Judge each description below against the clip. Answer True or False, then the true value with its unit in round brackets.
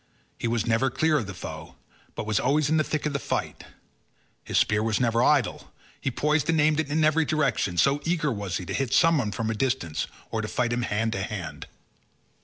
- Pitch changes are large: True (5.7 semitones)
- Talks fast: True (220 wpm)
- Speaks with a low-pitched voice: True (125 Hz)